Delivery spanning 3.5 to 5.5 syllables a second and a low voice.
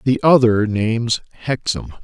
Yes: 4.4 syllables/s; low, 115 Hz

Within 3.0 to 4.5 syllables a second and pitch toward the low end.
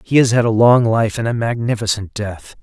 No: 5.2 syllables/s; low, 110 Hz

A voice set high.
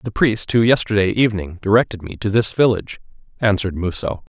No: low, 105 Hz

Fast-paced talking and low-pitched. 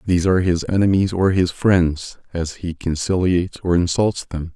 No: average, 170 wpm; very low, 90 Hz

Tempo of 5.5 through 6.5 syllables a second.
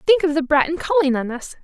Yes: 6.2 syllables/s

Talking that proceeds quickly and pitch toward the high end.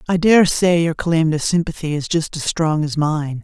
No: fast, 225 wpm; medium, 165 Hz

